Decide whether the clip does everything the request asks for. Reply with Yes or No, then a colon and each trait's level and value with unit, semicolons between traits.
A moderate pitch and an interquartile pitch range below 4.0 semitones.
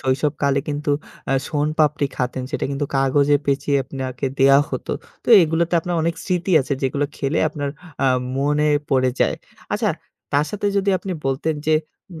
Yes: medium, 145 Hz; narrow, 2.5 semitones